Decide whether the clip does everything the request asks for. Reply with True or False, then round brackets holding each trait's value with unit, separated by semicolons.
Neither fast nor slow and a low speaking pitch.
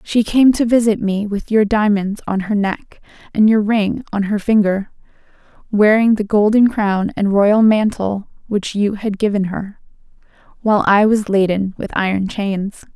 False (165 wpm; 205 Hz)